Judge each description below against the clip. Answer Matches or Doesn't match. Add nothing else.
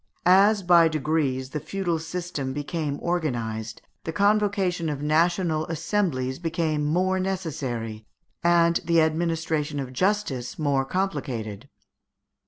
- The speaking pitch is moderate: Matches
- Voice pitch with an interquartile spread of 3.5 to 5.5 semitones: Matches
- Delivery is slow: Matches